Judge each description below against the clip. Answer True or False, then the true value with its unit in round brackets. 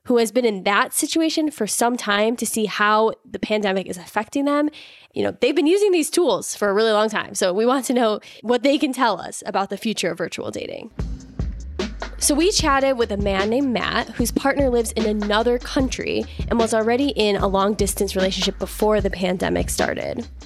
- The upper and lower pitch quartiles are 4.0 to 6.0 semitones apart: True (4.3 semitones)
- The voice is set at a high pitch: True (220 Hz)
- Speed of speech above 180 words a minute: True (205 wpm)